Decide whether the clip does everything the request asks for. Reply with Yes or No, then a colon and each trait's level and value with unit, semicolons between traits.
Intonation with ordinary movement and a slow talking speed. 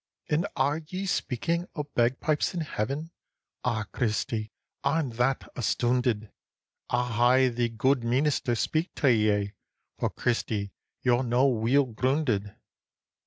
Yes: average, 3.9 semitones; slow, 120 wpm